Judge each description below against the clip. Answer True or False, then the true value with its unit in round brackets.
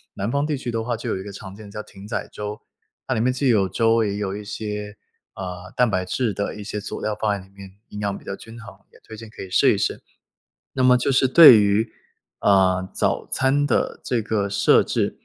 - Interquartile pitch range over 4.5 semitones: False (2.8 semitones)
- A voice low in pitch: True (105 Hz)